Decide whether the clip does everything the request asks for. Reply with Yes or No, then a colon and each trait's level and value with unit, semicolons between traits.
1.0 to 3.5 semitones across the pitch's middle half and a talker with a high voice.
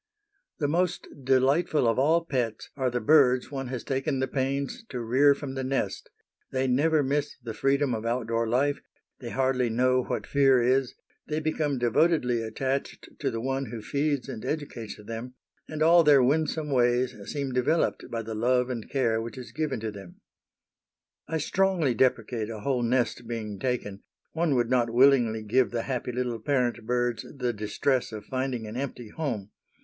No: average, 3.1 semitones; low, 130 Hz